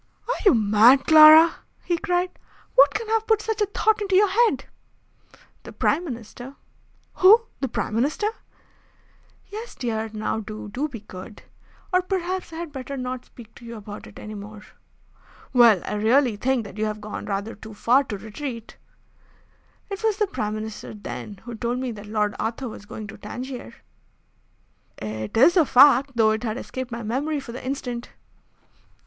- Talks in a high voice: Yes, high, 245 Hz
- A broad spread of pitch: Yes, wide, 6.7 semitones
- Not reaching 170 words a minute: No, average, 175 wpm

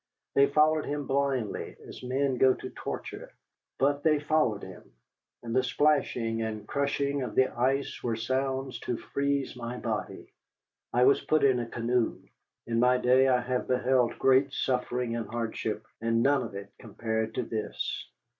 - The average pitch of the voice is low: Yes, low, 125 Hz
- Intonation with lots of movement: No, average, 3.1 semitones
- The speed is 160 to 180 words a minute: Yes, average, 165 wpm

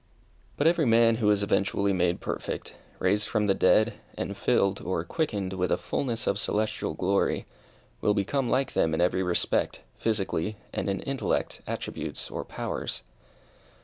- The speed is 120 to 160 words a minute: Yes, average, 155 wpm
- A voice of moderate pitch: No, low, 100 Hz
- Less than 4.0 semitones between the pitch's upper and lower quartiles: Yes, average, 3.4 semitones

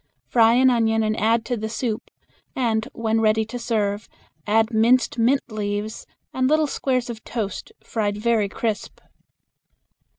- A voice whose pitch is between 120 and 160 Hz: No, high, 225 Hz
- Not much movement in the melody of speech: Yes, narrow, 1.8 semitones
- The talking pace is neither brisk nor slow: Yes, average, 145 wpm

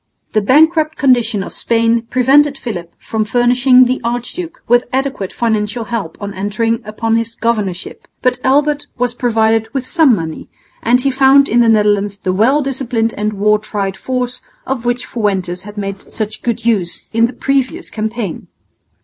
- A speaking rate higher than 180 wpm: No, average, 165 wpm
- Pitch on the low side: No, high, 230 Hz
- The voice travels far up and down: No, average, 3.3 semitones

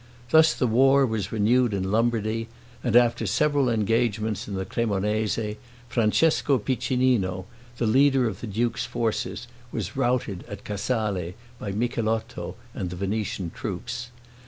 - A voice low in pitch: Yes, low, 115 Hz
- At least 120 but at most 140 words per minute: Yes, slow, 135 wpm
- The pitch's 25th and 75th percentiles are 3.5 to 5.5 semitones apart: No, average, 3.0 semitones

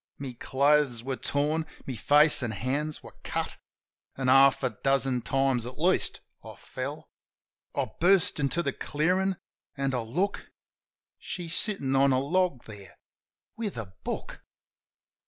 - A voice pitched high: No, medium, 140 Hz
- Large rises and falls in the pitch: No, average, 3.8 semitones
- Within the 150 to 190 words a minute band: No, average, 140 wpm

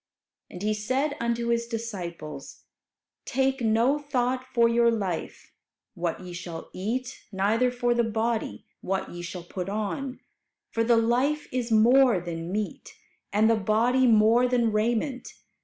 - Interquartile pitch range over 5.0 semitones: No, average, 3.7 semitones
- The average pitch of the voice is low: No, high, 230 Hz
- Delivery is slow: No, average, 145 wpm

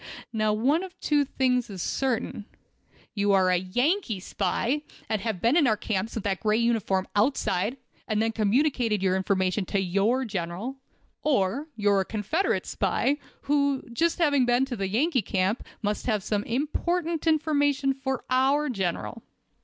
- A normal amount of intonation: No, wide, 5.7 semitones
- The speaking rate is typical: Yes, average, 160 wpm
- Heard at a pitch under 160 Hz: No, high, 230 Hz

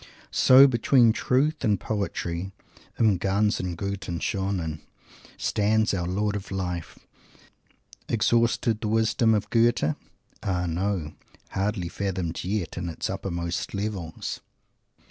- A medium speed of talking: No, slow, 110 wpm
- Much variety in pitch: No, average, 3.6 semitones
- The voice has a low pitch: Yes, low, 100 Hz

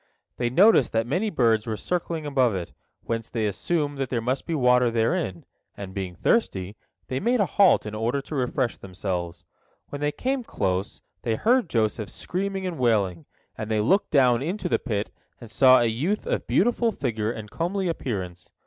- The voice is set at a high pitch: No, low, 125 Hz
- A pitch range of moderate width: No, wide, 7.8 semitones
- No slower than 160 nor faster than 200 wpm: Yes, average, 185 wpm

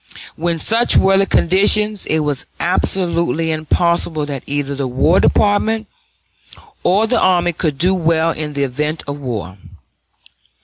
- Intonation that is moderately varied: Yes, average, 4.4 semitones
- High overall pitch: No, medium, 165 Hz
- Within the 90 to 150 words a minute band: Yes, average, 140 wpm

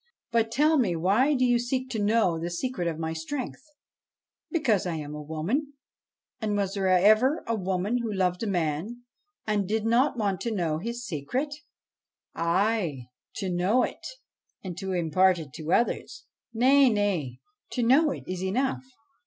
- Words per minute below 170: No, average, 180 wpm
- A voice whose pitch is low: No, high, 205 Hz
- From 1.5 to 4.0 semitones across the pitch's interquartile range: No, wide, 5.6 semitones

